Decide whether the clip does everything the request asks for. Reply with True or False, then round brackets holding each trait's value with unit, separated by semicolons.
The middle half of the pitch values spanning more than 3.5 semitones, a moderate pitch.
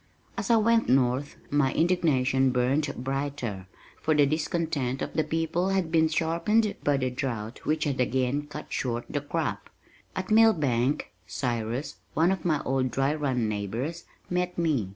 True (4.3 semitones; 145 Hz)